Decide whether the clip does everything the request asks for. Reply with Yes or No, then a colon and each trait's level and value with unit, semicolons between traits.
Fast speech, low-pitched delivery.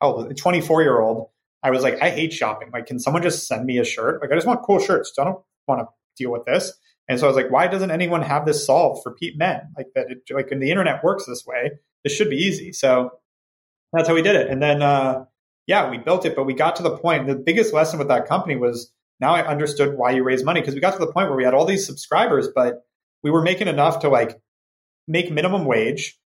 No: fast, 260 wpm; medium, 145 Hz